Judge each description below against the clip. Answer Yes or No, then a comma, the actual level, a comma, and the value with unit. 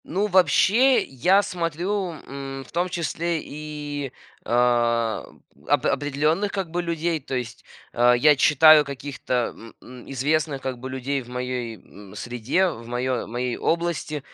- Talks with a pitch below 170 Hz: Yes, medium, 140 Hz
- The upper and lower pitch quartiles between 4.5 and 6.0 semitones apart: Yes, average, 5.3 semitones